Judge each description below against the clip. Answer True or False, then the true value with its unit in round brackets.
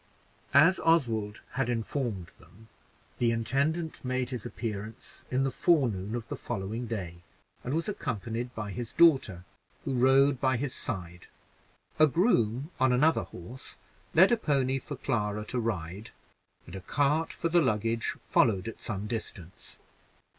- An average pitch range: True (4.5 semitones)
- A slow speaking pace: False (145 wpm)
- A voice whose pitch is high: False (120 Hz)